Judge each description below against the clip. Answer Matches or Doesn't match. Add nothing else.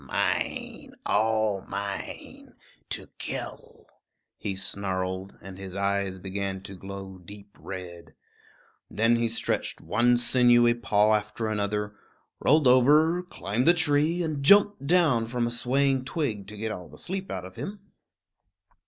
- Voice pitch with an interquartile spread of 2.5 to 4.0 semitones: Doesn't match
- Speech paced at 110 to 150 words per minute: Matches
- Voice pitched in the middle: Doesn't match